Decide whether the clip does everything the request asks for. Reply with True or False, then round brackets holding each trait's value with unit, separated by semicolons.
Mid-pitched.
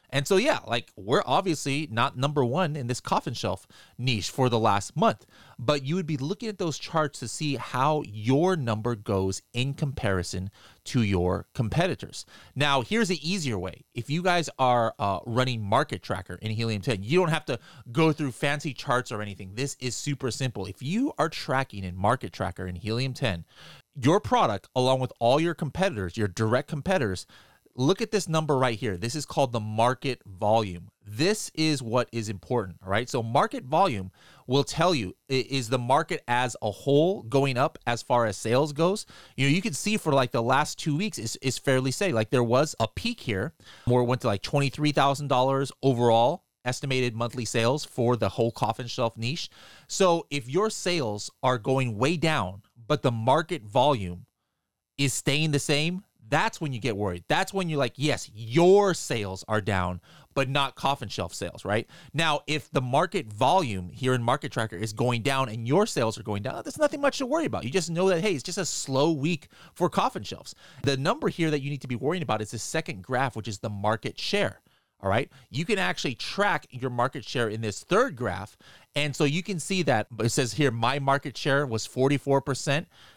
False (130 Hz)